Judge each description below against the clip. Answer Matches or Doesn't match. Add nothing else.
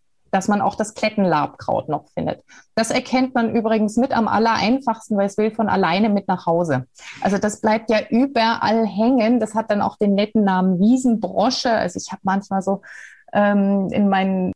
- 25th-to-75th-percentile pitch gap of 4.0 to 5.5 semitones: Doesn't match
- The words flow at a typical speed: Matches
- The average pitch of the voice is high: Matches